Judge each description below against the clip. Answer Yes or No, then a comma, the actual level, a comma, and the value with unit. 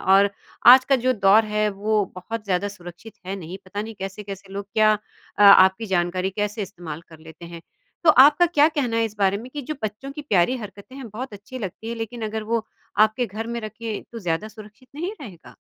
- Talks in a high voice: Yes, high, 215 Hz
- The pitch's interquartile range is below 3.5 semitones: Yes, average, 3.1 semitones